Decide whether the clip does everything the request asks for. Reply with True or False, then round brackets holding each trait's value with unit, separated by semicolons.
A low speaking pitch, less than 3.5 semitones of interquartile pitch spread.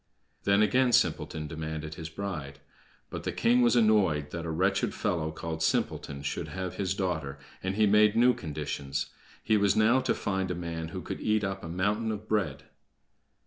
False (95 Hz; 5.1 semitones)